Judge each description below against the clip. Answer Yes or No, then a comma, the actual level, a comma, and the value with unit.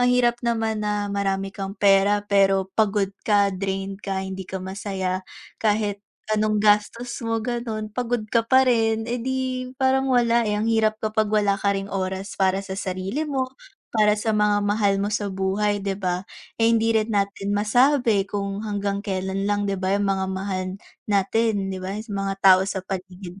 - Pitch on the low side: No, high, 205 Hz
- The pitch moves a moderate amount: No, narrow, 2.3 semitones